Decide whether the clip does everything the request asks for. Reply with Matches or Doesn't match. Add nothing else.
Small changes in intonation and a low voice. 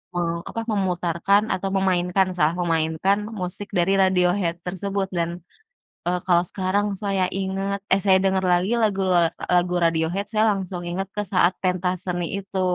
Doesn't match